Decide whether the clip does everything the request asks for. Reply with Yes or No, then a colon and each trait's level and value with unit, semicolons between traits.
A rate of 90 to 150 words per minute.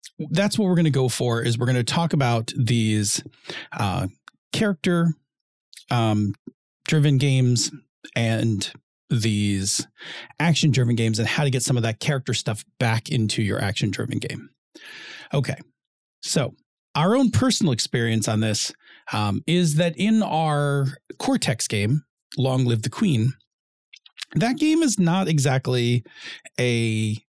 Yes: average, 140 wpm